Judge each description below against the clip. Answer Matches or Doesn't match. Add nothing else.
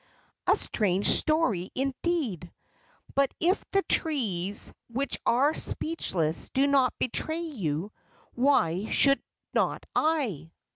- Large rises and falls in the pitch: Matches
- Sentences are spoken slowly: Matches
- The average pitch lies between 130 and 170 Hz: Doesn't match